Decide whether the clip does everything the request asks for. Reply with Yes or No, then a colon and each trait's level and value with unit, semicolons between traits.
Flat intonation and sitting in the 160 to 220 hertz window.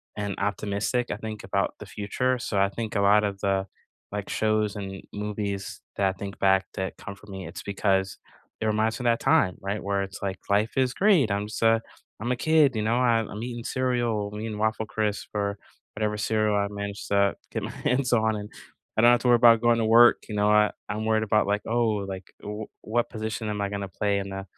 No: narrow, 2.0 semitones; low, 105 Hz